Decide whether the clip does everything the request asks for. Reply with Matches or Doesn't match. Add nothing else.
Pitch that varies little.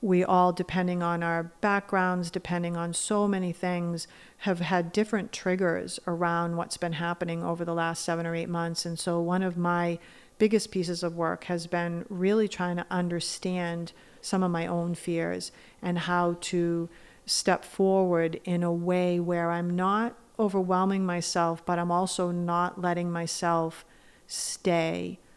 Matches